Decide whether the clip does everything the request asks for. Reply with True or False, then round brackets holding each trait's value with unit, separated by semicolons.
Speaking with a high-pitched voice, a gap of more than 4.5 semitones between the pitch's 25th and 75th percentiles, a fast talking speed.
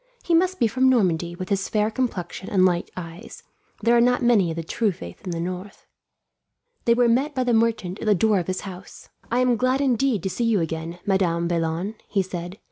True (200 Hz; 5.2 semitones; 220 wpm)